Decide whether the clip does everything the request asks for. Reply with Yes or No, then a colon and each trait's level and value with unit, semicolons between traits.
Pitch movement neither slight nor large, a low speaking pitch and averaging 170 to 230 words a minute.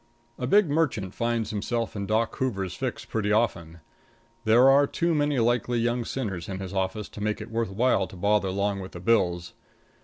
Yes: average, 4.0 semitones; low, 110 Hz; average, 190 wpm